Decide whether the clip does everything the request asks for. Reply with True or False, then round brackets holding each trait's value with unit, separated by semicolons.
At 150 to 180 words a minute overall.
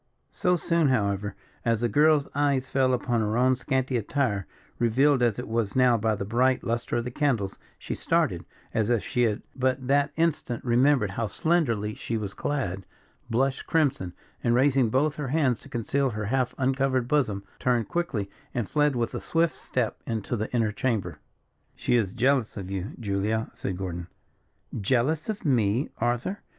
True (175 wpm)